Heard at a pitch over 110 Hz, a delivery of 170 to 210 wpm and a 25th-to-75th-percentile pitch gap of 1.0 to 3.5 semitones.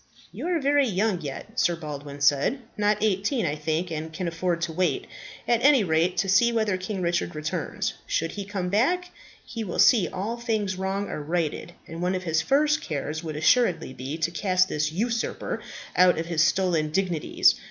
No: medium, 185 Hz; average, 190 wpm; average, 5.2 semitones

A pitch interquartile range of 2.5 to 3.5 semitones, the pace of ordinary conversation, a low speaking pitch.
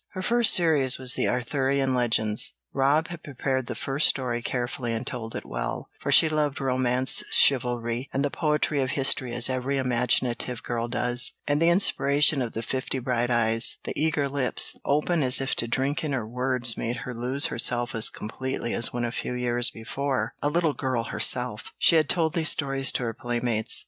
Yes: average, 2.8 semitones; average, 190 wpm; low, 130 Hz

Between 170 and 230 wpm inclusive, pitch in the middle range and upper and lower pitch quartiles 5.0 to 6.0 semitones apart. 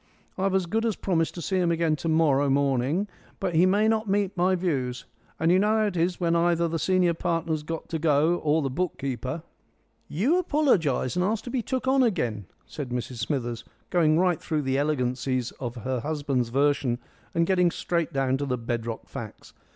Yes: average, 200 wpm; medium, 165 Hz; wide, 5.4 semitones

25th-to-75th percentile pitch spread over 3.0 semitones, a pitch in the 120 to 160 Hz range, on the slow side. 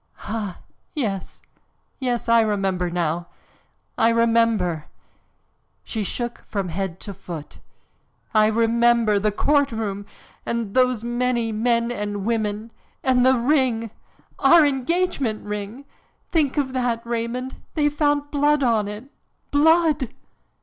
No: average, 3.9 semitones; high, 230 Hz; slow, 115 wpm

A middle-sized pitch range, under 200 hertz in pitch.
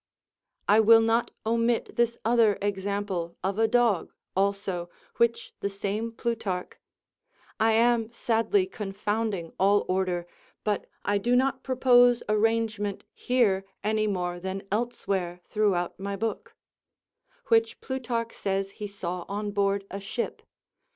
No: average, 3.0 semitones; high, 210 Hz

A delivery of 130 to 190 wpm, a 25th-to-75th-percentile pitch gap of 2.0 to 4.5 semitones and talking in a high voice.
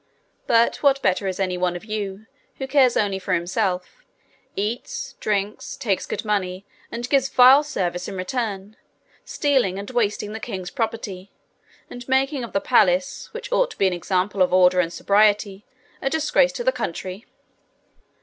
No: average, 165 wpm; average, 5.1 semitones; high, 210 Hz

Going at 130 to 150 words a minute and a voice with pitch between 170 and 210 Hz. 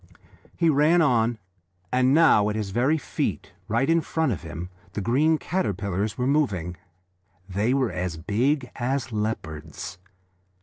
No: average, 140 wpm; low, 115 Hz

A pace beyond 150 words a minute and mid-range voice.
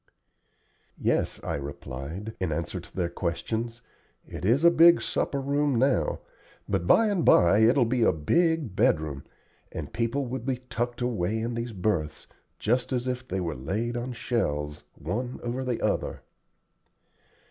No: average, 160 wpm; low, 115 Hz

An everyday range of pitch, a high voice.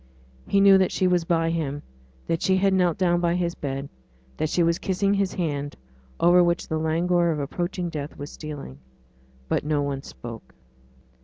No: average, 3.4 semitones; medium, 170 Hz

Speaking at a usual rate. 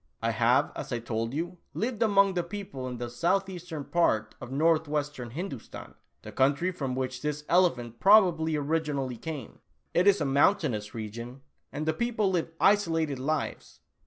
Yes: average, 160 wpm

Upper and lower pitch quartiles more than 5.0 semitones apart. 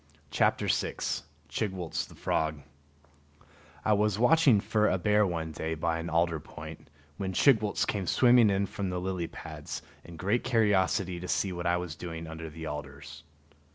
No: average, 4.1 semitones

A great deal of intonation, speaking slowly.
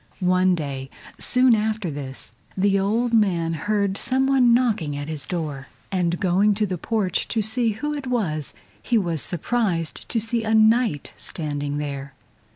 No: wide, 6.2 semitones; average, 160 wpm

